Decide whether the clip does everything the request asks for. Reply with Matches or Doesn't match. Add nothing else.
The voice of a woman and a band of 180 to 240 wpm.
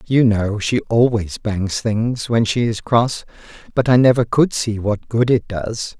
Doesn't match